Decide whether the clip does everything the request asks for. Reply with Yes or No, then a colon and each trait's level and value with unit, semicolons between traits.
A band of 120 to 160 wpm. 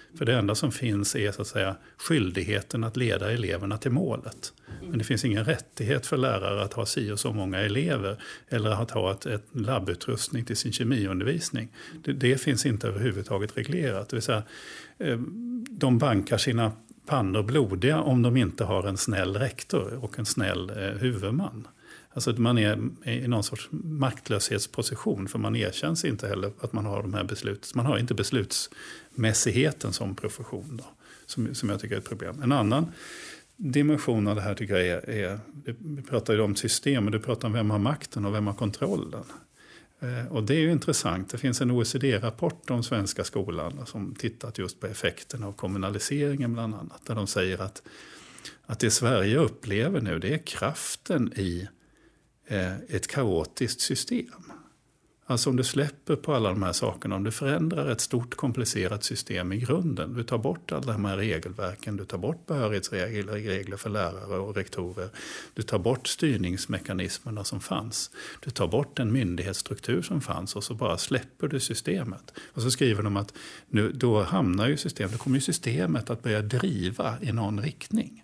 No: average, 175 wpm